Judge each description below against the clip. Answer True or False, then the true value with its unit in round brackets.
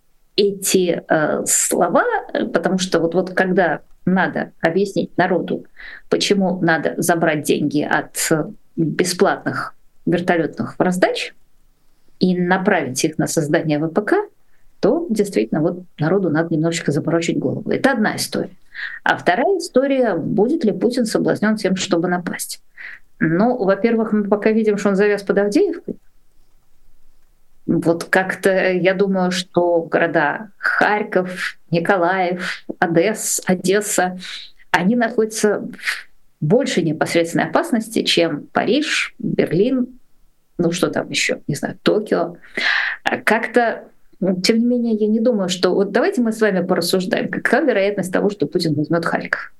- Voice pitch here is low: False (185 Hz)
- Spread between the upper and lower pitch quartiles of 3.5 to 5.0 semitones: True (4.1 semitones)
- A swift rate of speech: False (125 wpm)